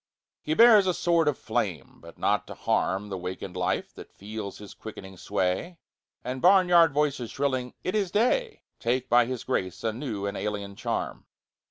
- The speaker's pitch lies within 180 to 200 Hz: No, low, 125 Hz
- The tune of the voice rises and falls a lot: Yes, wide, 9.0 semitones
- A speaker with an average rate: Yes, average, 175 wpm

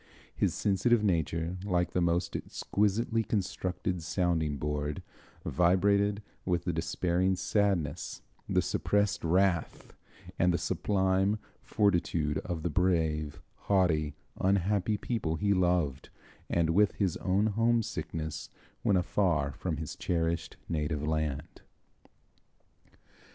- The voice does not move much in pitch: No, average, 3.7 semitones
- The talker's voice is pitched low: Yes, very low, 90 Hz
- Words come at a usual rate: No, slow, 110 wpm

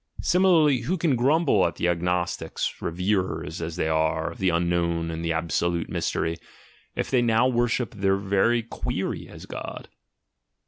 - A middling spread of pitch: No, wide, 6.2 semitones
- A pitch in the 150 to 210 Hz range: No, very low, 95 Hz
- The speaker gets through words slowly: No, average, 150 wpm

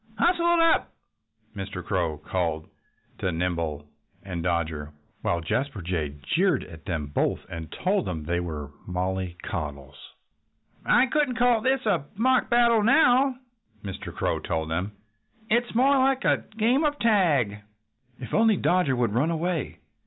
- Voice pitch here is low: Yes, low, 110 Hz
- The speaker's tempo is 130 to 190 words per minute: Yes, average, 145 wpm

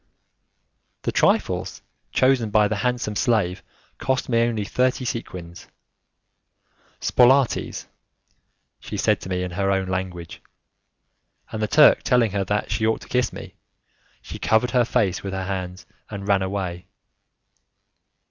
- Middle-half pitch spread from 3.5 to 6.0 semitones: Yes, average, 4.4 semitones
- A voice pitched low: Yes, low, 105 Hz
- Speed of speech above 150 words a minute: No, average, 140 wpm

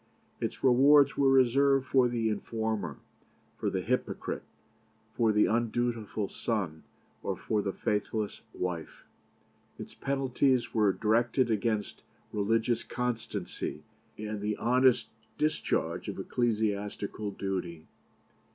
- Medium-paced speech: No, slow, 105 wpm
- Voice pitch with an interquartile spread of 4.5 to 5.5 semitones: No, average, 3.0 semitones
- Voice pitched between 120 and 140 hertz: No, low, 110 Hz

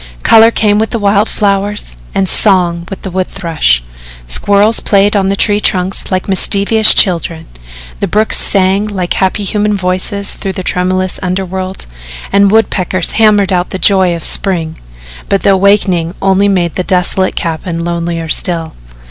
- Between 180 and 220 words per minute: No, average, 155 wpm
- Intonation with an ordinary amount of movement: No, narrow, 2.1 semitones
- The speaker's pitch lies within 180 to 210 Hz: Yes, high, 190 Hz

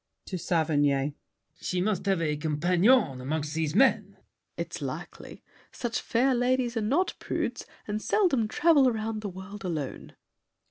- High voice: Yes, high, 200 Hz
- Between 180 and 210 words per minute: No, average, 145 wpm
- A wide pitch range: Yes, wide, 7.2 semitones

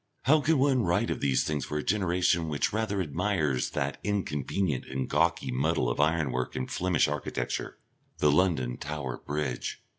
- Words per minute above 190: No, average, 160 wpm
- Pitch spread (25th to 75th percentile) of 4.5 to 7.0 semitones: Yes, average, 5.1 semitones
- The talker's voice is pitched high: No, very low, 75 Hz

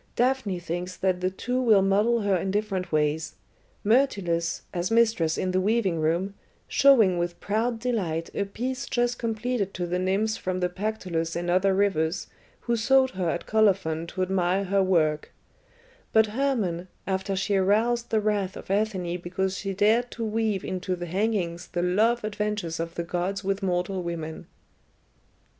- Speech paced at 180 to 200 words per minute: No, average, 165 wpm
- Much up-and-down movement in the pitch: No, average, 3.6 semitones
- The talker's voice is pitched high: Yes, high, 195 Hz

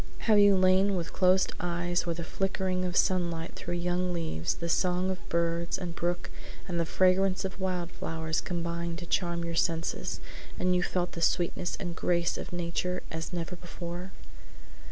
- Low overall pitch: No, medium, 175 Hz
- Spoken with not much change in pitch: Yes, narrow, 1.4 semitones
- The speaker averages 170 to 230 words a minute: Yes, average, 175 wpm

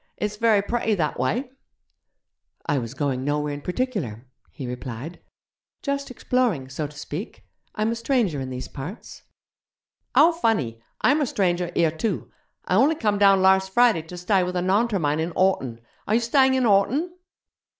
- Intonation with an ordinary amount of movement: No, wide, 7.8 semitones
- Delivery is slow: No, average, 165 wpm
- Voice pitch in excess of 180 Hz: Yes, high, 190 Hz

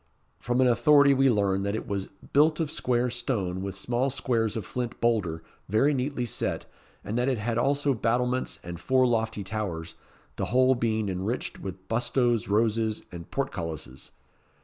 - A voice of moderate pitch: No, low, 115 Hz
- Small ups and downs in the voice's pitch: No, average, 4.1 semitones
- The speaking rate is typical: Yes, average, 165 wpm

